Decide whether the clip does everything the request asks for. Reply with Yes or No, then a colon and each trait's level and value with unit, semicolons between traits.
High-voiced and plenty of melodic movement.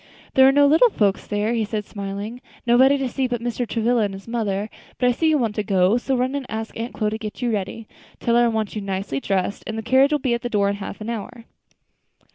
No: high, 230 Hz; average, 3.1 semitones